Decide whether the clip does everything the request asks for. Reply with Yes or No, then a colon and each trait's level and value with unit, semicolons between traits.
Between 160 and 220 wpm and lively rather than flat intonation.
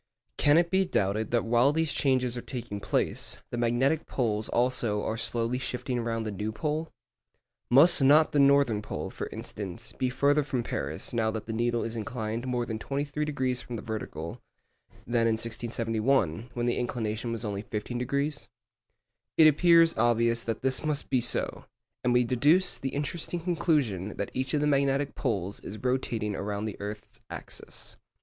No: average, 170 wpm; average, 4.1 semitones